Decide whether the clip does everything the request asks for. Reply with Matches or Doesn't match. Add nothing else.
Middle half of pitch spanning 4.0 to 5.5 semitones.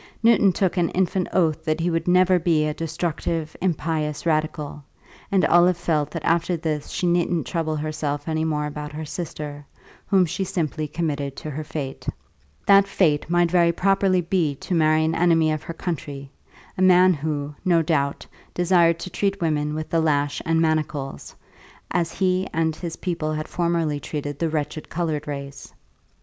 Doesn't match